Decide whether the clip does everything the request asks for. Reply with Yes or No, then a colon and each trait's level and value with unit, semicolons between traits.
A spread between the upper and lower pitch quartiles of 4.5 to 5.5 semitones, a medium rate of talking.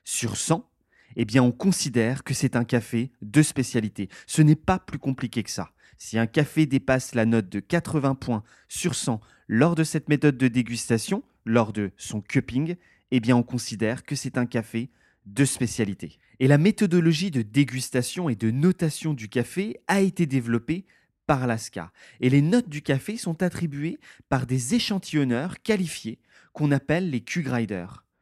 Yes: average, 5.1 semitones; average, 170 wpm